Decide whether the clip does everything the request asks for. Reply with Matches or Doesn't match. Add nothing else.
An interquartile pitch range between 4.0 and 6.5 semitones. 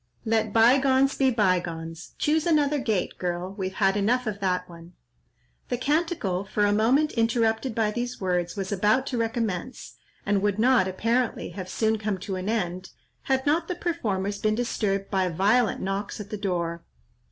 Matches